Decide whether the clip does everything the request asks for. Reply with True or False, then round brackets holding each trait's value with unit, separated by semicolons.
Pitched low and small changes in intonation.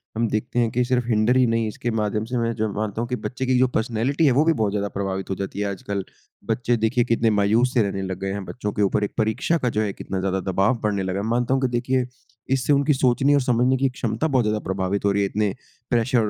False (115 Hz; 3.7 semitones)